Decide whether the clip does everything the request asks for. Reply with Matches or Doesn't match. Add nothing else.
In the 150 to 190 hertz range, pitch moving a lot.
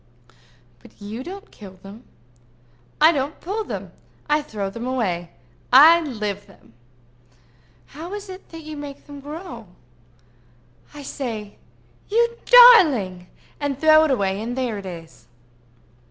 Doesn't match